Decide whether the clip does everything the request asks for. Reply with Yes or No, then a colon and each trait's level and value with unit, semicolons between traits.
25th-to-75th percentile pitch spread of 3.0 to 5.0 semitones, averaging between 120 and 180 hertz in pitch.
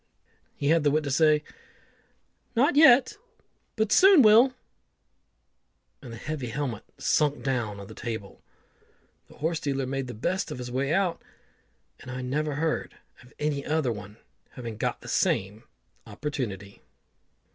Yes: average, 4.7 semitones; medium, 140 Hz